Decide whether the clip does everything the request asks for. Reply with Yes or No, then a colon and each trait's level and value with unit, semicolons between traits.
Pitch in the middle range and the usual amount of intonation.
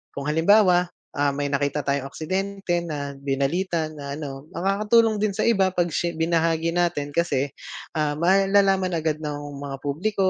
Yes: medium, 165 Hz; average, 4.7 semitones